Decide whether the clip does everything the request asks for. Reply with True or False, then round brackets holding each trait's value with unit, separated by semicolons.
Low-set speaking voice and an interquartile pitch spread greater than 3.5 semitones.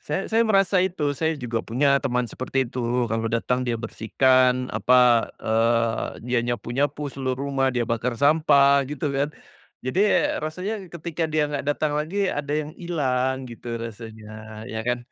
True (130 Hz; 4.0 semitones)